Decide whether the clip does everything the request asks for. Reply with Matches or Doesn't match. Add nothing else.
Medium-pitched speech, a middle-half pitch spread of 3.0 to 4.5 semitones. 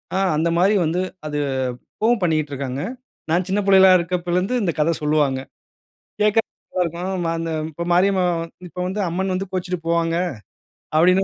Doesn't match